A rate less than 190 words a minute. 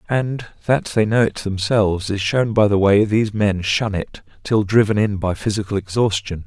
No: average, 195 wpm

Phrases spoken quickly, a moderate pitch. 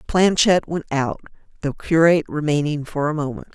No: average, 150 wpm; medium, 155 Hz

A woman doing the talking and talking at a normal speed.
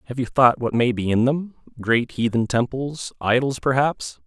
No: male; average, 170 wpm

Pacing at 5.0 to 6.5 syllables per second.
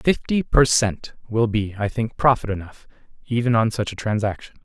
Yes: 5.1 syllables/s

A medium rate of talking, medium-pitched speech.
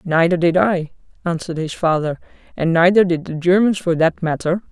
Yes: average, 180 wpm; medium, 170 Hz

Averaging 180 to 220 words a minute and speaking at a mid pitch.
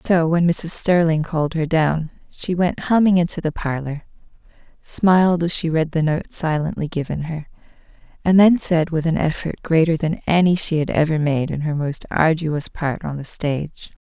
Yes: average, 185 wpm; medium, 160 Hz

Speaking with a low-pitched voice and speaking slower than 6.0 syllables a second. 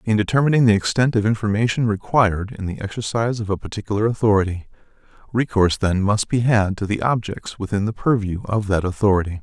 No: low, 105 Hz; 6.3 syllables/s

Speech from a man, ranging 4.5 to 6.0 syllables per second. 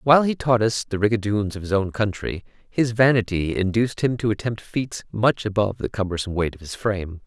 Yes: male; 5.6 syllables/s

